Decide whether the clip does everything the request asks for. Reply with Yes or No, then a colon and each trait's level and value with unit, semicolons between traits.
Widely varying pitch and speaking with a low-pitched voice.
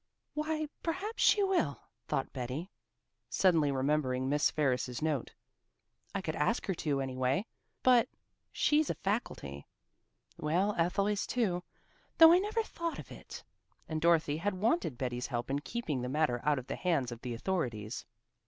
No: wide, 8.1 semitones; medium, 155 Hz